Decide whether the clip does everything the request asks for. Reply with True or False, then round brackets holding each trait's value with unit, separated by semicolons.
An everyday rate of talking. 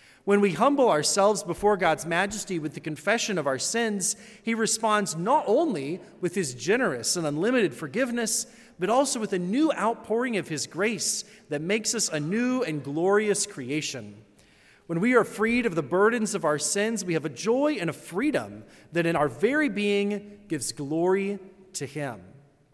True (175 wpm)